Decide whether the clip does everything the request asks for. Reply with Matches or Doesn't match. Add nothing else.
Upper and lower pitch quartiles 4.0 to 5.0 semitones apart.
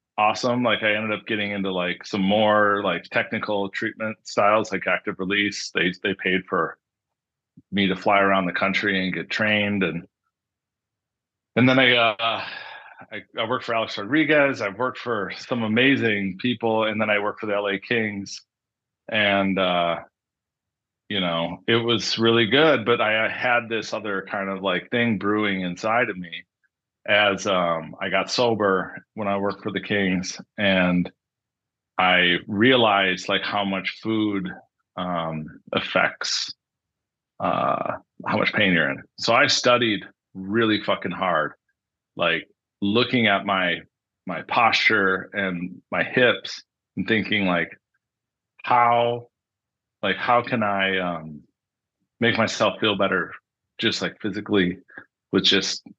Doesn't match